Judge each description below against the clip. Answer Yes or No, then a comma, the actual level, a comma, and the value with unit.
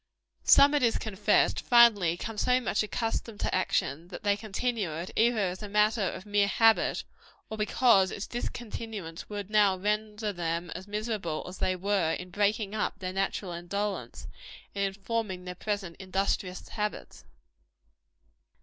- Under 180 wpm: Yes, average, 155 wpm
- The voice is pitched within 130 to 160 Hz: No, high, 205 Hz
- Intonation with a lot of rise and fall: No, average, 2.7 semitones